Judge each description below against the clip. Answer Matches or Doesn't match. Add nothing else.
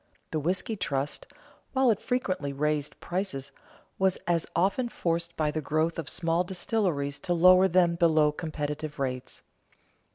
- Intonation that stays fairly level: Doesn't match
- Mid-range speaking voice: Matches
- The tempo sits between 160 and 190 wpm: Doesn't match